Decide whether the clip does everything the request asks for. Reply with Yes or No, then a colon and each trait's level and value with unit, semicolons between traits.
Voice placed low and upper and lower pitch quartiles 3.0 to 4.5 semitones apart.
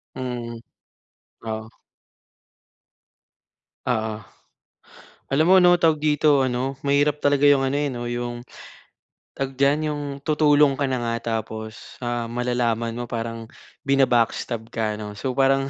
Yes: low, 125 Hz; average, 3.3 semitones